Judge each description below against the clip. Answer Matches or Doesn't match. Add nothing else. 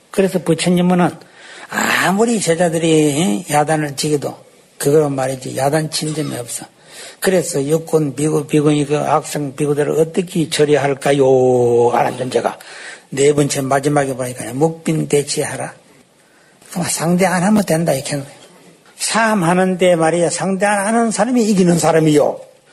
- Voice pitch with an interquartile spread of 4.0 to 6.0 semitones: Doesn't match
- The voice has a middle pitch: Matches